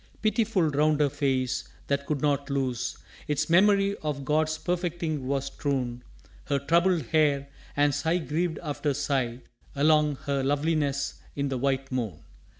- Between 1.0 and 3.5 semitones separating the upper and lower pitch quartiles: Yes, narrow, 2.5 semitones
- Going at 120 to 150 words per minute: Yes, average, 145 wpm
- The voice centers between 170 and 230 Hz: No, medium, 145 Hz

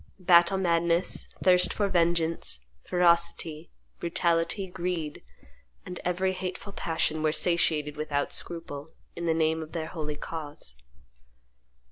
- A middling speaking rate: No, slow, 115 wpm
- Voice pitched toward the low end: No, medium, 170 Hz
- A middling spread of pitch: No, narrow, 2.2 semitones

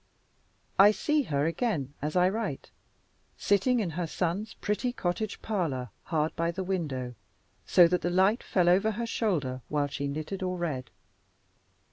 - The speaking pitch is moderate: Yes, medium, 180 Hz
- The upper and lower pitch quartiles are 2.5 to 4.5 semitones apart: No, average, 5.2 semitones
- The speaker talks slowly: No, average, 155 wpm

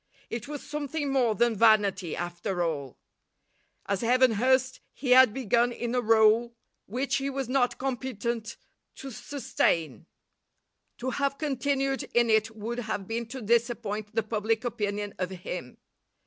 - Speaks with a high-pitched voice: Yes, high, 235 Hz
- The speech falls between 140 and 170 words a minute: Yes, average, 145 wpm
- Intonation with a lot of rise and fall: No, average, 3.8 semitones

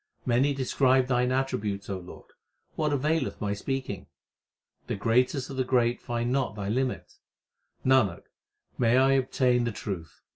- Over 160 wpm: No, average, 145 wpm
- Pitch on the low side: Yes, low, 125 Hz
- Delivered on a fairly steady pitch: No, average, 3.4 semitones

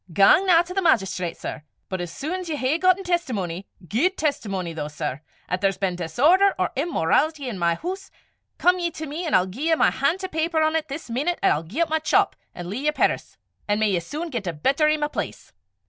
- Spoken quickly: Yes, fast, 240 wpm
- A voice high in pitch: Yes, very high, 290 Hz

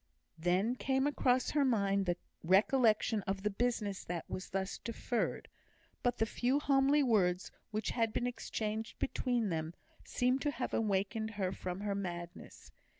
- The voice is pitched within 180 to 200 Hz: No, high, 215 Hz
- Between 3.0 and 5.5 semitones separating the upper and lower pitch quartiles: Yes, average, 4.4 semitones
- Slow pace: No, average, 150 wpm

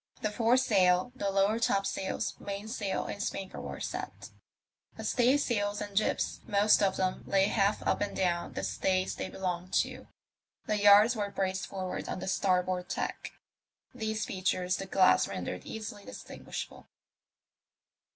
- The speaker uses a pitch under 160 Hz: No, high, 195 Hz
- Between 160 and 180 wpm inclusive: No, average, 150 wpm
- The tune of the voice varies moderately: No, narrow, 2.2 semitones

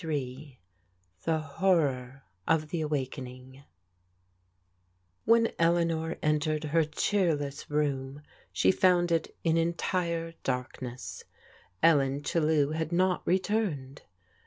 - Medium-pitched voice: Yes, medium, 155 Hz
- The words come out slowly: Yes, slow, 100 wpm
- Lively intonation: No, average, 3.3 semitones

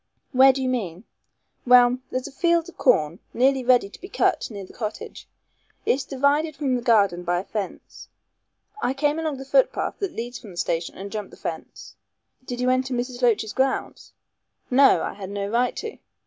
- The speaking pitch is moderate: No, very high, 250 Hz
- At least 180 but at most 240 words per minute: Yes, average, 195 wpm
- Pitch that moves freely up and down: No, average, 4.5 semitones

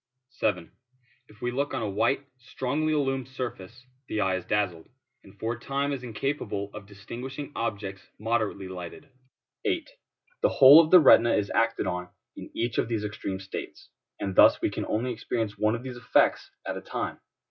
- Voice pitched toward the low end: Yes, low, 115 Hz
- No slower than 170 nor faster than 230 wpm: Yes, average, 180 wpm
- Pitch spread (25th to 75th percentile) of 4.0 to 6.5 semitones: Yes, average, 4.6 semitones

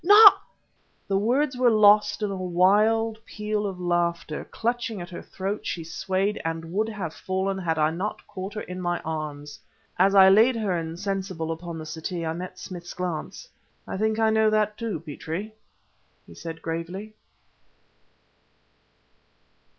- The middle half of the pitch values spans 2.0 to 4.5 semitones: Yes, average, 4.1 semitones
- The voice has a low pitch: No, high, 190 Hz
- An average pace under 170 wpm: Yes, average, 160 wpm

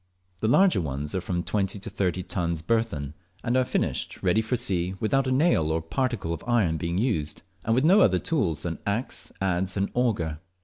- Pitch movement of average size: No, wide, 6.4 semitones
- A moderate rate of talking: Yes, average, 195 wpm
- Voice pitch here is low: Yes, very low, 95 Hz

